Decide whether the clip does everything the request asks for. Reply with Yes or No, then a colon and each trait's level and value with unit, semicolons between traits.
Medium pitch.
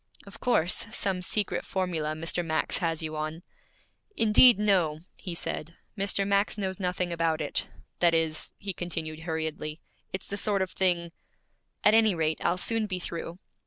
Yes: medium, 175 Hz